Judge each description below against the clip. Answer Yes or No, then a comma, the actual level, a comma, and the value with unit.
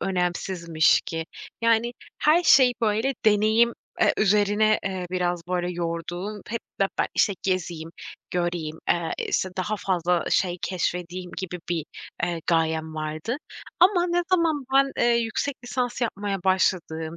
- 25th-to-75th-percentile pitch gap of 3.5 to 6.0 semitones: Yes, average, 4.8 semitones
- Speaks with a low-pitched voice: No, medium, 185 Hz